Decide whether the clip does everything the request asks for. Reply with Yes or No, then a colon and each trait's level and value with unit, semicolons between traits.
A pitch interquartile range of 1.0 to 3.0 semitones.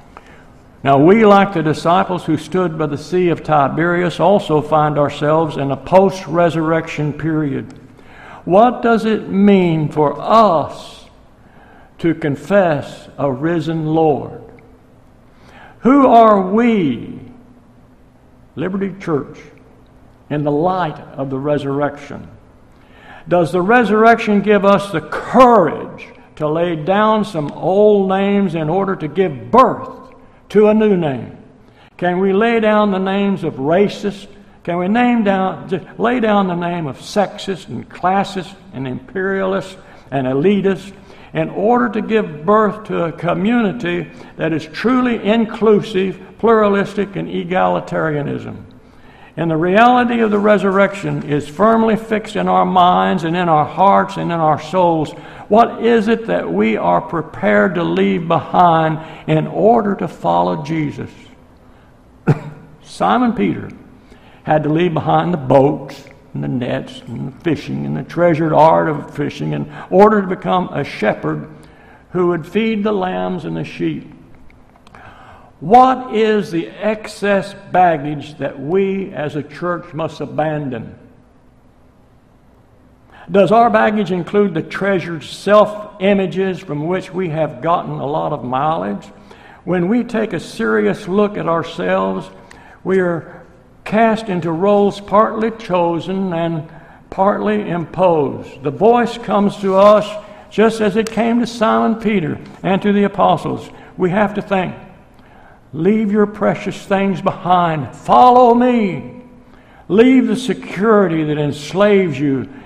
No: average, 5.0 semitones